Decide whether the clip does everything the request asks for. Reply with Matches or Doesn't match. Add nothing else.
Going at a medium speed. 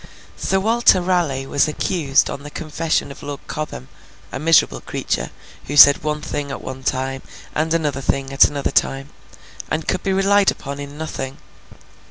Matches